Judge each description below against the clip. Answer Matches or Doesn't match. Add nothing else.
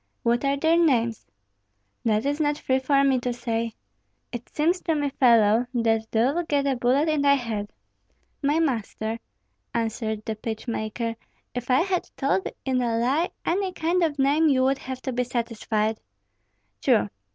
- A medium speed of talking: Matches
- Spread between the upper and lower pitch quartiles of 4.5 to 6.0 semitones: Doesn't match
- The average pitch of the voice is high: Matches